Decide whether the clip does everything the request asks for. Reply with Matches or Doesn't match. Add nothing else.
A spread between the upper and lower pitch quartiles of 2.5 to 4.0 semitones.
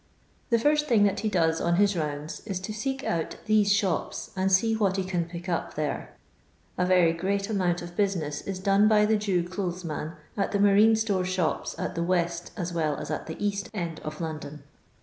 Matches